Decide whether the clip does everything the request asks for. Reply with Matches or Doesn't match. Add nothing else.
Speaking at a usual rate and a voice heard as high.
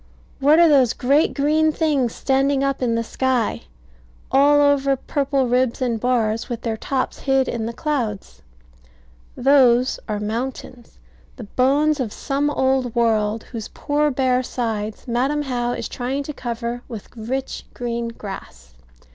Matches